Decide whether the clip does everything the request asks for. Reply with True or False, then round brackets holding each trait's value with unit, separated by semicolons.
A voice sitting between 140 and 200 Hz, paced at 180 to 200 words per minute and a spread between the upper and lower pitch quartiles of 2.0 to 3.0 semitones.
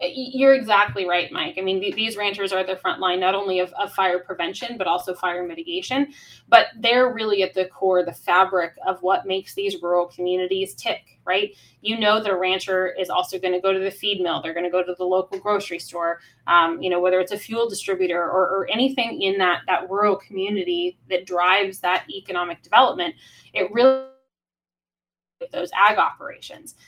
True (190 Hz; 190 wpm; 2.4 semitones)